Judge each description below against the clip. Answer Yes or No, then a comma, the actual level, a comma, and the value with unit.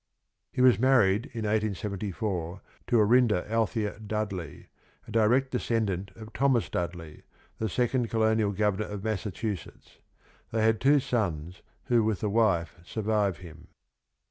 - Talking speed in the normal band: No, slow, 130 wpm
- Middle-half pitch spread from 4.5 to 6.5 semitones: No, average, 3.0 semitones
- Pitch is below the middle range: Yes, low, 110 Hz